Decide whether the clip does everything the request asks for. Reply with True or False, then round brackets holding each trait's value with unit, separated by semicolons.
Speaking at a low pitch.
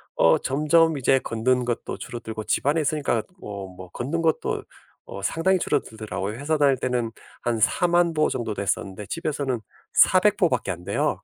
True (130 Hz)